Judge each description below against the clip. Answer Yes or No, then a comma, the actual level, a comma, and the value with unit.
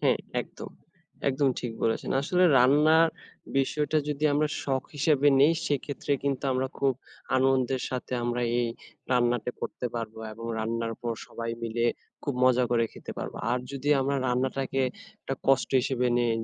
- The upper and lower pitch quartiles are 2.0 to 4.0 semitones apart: Yes, narrow, 2.6 semitones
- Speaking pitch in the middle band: No, low, 130 Hz